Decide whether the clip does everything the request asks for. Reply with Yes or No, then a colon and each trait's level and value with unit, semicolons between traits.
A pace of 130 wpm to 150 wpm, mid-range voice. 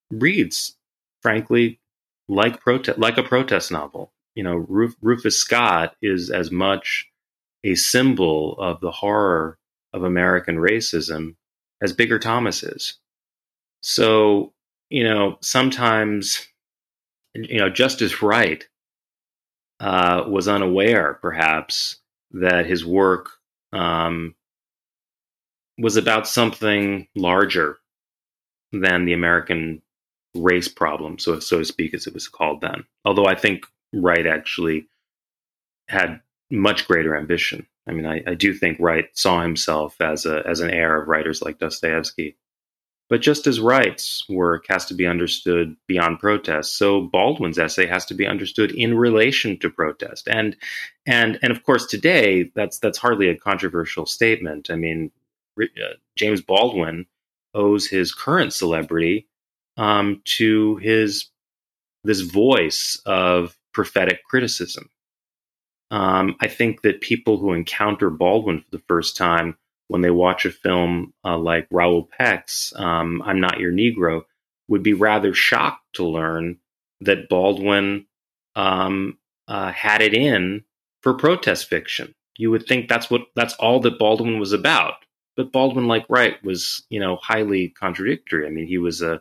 No: average, 140 wpm; very low, 95 Hz